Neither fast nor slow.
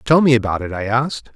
No: fast, 265 wpm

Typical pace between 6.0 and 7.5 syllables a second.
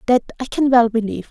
Yes: 7.1 syllables/s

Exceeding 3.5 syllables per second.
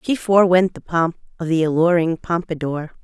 Yes: 5.5 syllables/s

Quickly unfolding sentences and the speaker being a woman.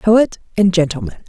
No: average, 140 wpm; female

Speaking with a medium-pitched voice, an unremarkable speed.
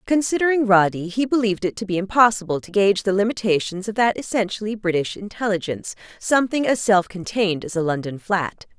No: high, 200 Hz; average, 155 wpm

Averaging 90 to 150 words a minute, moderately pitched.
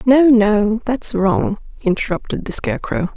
No: slow, 135 wpm; high, 225 Hz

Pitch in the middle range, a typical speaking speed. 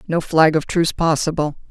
Yes: medium, 160 Hz; average, 175 wpm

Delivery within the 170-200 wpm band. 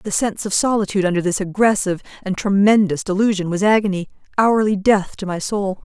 Yes: average, 175 wpm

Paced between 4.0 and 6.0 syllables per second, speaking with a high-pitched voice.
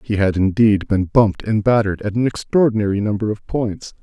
No: 5.7 syllables/s; low, 105 Hz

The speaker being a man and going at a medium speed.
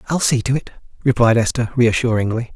Yes: male; average, 165 wpm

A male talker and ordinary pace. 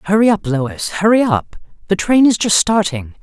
No: female; average, 185 wpm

